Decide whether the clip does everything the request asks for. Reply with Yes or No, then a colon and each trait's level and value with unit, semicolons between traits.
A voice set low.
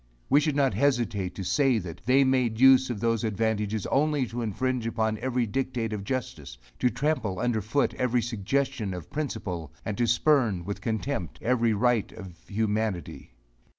Yes: low, 115 Hz